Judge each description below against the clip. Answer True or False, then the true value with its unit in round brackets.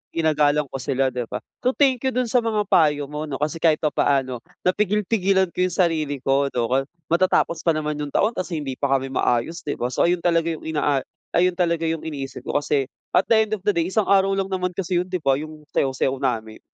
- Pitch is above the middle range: False (160 Hz)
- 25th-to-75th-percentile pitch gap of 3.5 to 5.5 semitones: True (5.0 semitones)